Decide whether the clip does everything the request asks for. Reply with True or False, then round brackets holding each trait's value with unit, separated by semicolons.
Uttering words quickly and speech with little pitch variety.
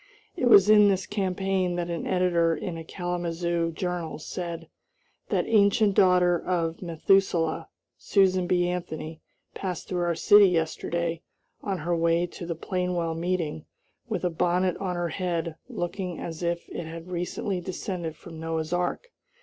False (150 wpm; 1.7 semitones)